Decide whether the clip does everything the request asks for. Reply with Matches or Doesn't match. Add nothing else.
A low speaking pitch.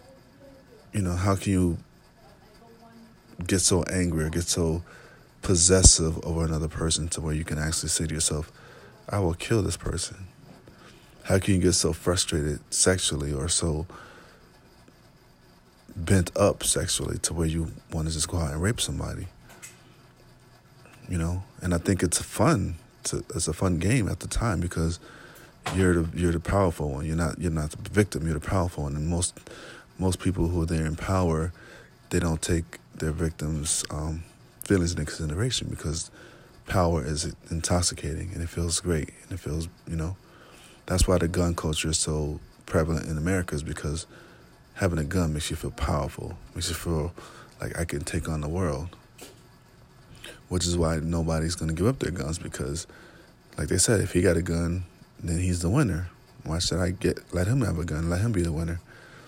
Matches